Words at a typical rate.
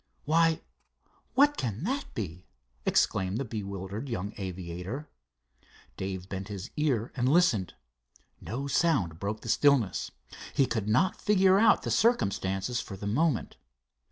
No: slow, 130 wpm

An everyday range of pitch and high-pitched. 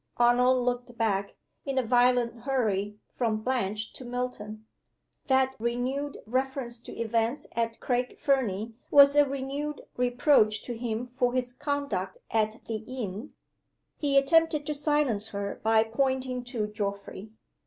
Yes: average, 3.3 semitones; high, 245 Hz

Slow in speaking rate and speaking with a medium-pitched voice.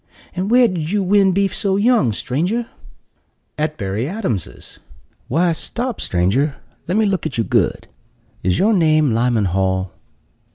No: average, 150 wpm; medium, 160 Hz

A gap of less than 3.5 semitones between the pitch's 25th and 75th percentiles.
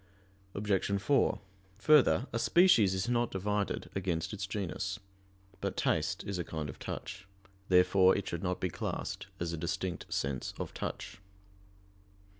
Yes: narrow, 2.6 semitones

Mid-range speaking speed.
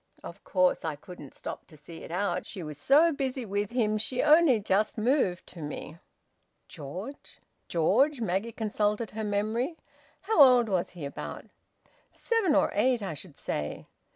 Yes: average, 160 wpm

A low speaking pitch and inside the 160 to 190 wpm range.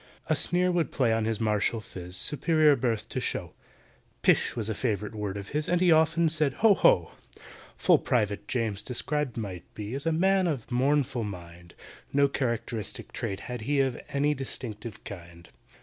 Yes: low, 120 Hz; average, 180 wpm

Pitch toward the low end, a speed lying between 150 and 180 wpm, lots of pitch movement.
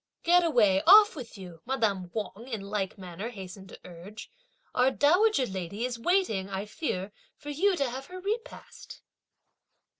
No: high, 230 Hz; average, 155 wpm; wide, 8.1 semitones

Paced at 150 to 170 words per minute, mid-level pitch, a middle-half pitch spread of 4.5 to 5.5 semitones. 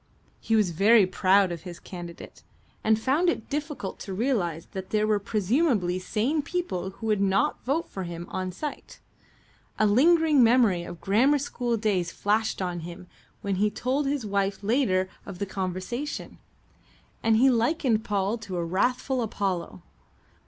No: average, 160 wpm; high, 210 Hz; average, 5.2 semitones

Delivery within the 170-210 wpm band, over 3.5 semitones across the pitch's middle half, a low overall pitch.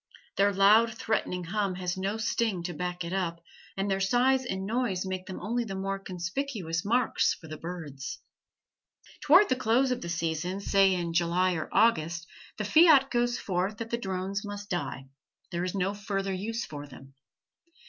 No: average, 180 wpm; average, 4.1 semitones; high, 195 Hz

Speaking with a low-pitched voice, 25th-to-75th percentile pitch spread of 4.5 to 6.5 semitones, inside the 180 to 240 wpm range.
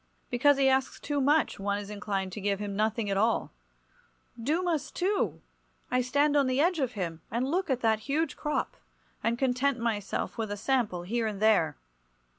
No: high, 235 Hz; wide, 5.4 semitones; average, 185 wpm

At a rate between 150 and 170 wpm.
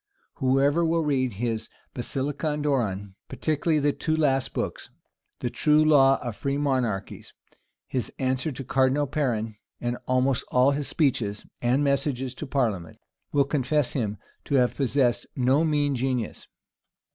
No: average, 140 wpm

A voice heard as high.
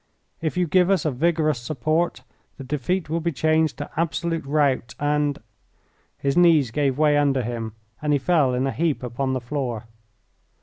No: medium, 150 Hz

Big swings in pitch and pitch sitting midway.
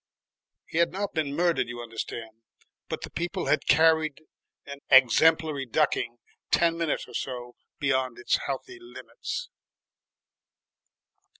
No: average, 4.6 semitones; medium, 150 Hz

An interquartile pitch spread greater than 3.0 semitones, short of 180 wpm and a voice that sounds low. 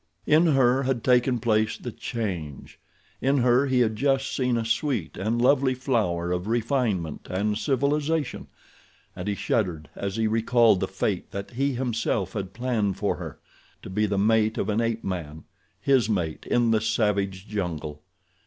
Yes: average, 4.4 semitones; average, 160 wpm; low, 115 Hz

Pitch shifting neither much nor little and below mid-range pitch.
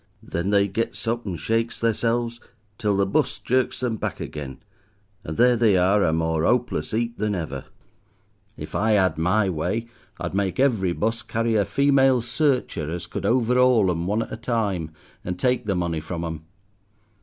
Yes: average, 5.0 semitones; low, 105 Hz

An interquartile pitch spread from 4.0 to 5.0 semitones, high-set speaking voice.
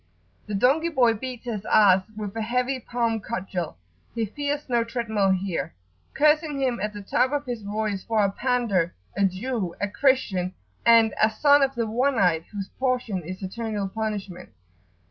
Yes: average, 4.3 semitones; high, 220 Hz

